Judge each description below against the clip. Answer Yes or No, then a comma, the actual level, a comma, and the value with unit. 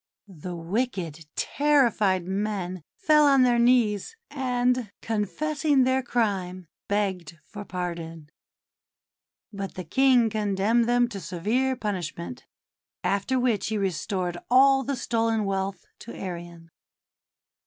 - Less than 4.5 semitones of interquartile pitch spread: No, average, 5.3 semitones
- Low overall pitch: No, high, 210 Hz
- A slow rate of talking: Yes, slow, 115 wpm